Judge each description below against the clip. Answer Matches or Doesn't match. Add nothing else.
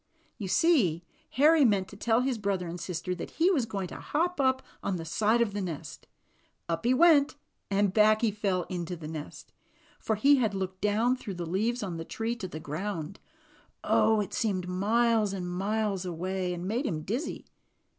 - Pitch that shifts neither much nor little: Matches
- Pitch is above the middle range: Matches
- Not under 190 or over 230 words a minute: Matches